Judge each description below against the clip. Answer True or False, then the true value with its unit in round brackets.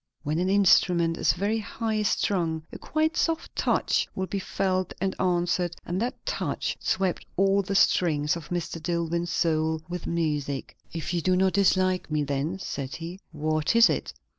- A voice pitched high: False (175 Hz)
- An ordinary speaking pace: True (170 wpm)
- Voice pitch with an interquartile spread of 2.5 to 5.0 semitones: True (3.1 semitones)